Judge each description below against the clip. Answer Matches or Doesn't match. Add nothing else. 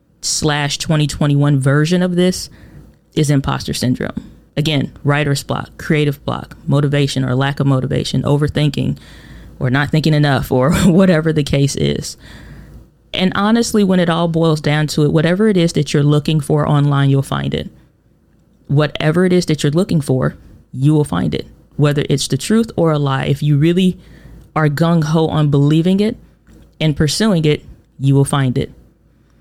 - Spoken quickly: Doesn't match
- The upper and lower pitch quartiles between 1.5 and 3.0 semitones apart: Matches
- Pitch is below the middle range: Doesn't match